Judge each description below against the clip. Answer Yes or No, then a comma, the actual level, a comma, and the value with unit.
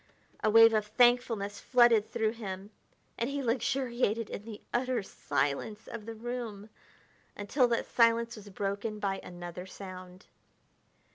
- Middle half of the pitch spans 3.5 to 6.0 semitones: No, average, 2.9 semitones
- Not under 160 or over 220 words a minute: No, slow, 135 wpm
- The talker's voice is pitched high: Yes, high, 220 Hz